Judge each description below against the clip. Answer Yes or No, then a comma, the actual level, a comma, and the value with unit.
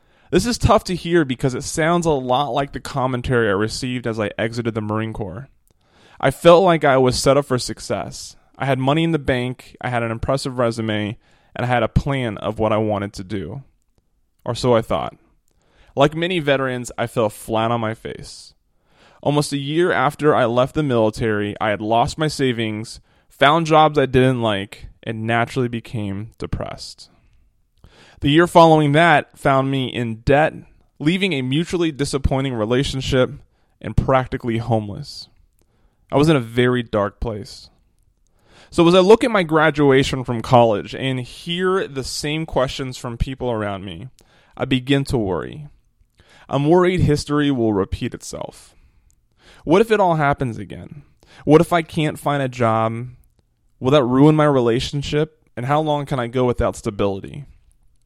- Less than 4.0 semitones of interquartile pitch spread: No, average, 4.5 semitones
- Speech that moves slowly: No, average, 170 wpm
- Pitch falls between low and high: No, low, 130 Hz